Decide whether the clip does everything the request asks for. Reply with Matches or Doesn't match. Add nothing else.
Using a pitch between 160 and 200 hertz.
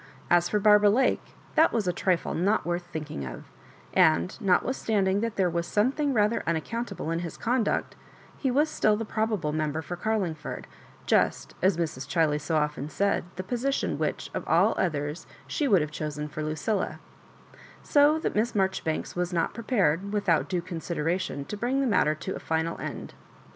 Matches